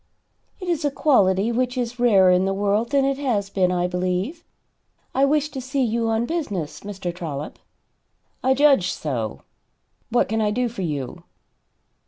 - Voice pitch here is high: Yes, high, 225 Hz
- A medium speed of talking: Yes, average, 170 wpm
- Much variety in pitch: Yes, wide, 6.3 semitones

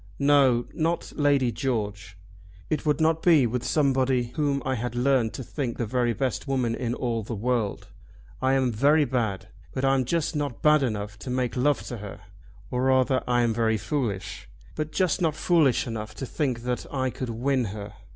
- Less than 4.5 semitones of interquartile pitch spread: Yes, average, 3.2 semitones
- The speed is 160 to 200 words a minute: Yes, average, 190 wpm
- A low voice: Yes, low, 130 Hz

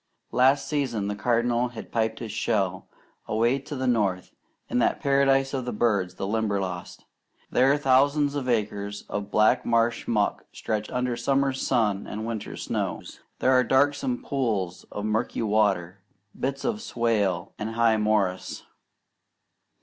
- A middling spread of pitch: Yes, average, 4.1 semitones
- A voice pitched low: Yes, low, 115 Hz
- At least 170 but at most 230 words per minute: No, average, 145 wpm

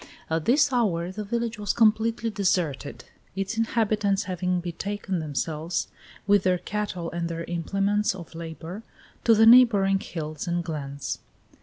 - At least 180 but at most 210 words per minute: No, average, 140 wpm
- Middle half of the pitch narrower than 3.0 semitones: No, average, 4.0 semitones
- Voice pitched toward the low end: No, high, 190 Hz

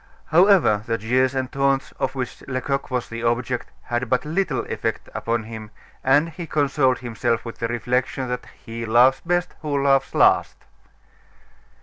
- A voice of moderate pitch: No, low, 130 Hz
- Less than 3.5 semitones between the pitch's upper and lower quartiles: Yes, average, 2.8 semitones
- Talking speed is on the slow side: No, average, 155 wpm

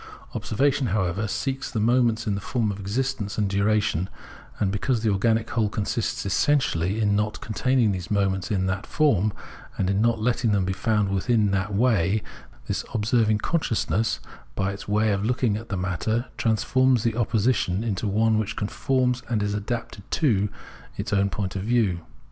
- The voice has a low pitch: Yes, low, 105 Hz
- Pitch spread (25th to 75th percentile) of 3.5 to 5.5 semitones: No, average, 2.9 semitones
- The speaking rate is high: No, average, 175 wpm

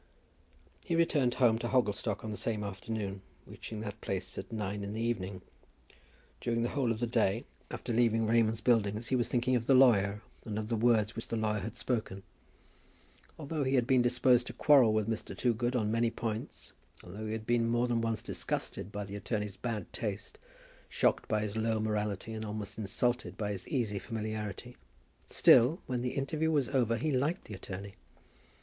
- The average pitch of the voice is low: Yes, low, 115 Hz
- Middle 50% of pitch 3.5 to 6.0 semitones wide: No, narrow, 2.6 semitones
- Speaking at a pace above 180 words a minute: Yes, average, 190 wpm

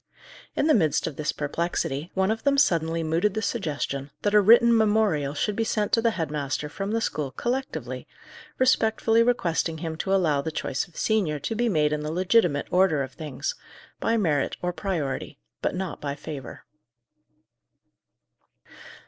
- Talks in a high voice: No, medium, 175 Hz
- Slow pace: No, average, 170 wpm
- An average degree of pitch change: No, wide, 6.4 semitones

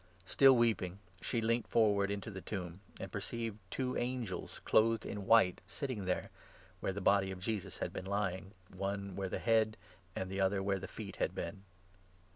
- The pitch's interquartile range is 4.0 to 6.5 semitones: No, average, 2.8 semitones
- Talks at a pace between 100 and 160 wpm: No, average, 190 wpm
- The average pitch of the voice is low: Yes, low, 100 Hz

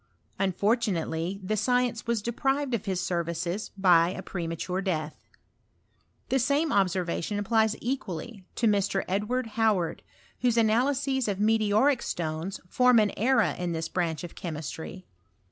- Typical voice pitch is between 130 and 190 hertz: No, high, 200 Hz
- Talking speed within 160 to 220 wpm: No, slow, 135 wpm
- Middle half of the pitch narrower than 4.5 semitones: No, average, 5.0 semitones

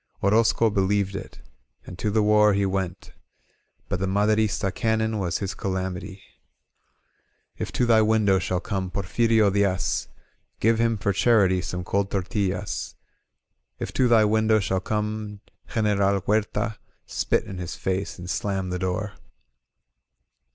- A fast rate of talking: No, slow, 135 wpm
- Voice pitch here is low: Yes, low, 100 Hz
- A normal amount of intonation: No, narrow, 2.3 semitones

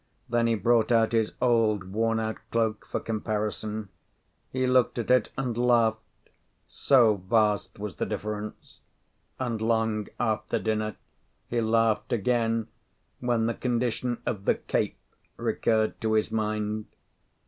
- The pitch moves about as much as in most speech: No, narrow, 1.6 semitones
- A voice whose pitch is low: Yes, low, 110 Hz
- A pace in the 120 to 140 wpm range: Yes, slow, 135 wpm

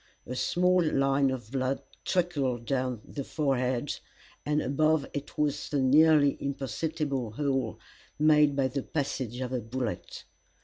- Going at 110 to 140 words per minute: Yes, slow, 135 wpm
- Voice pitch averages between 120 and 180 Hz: Yes, low, 135 Hz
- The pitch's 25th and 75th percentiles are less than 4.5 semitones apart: Yes, narrow, 2.6 semitones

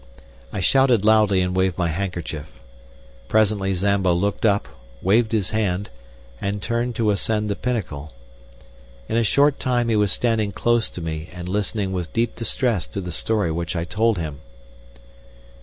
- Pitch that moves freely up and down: No, average, 3.8 semitones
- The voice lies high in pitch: No, low, 100 Hz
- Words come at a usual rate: Yes, average, 160 wpm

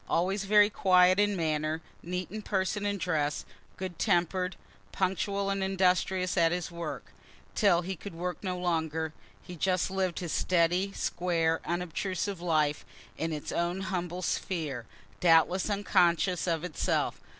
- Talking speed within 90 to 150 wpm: Yes, average, 140 wpm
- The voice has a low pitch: No, medium, 180 Hz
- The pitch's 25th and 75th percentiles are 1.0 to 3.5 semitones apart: Yes, narrow, 2.4 semitones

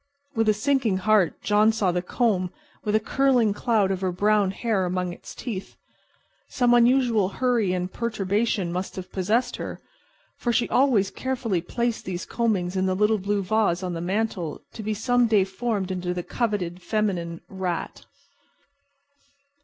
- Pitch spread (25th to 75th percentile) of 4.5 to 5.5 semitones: No, average, 3.7 semitones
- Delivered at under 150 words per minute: No, average, 160 wpm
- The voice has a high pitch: Yes, high, 205 Hz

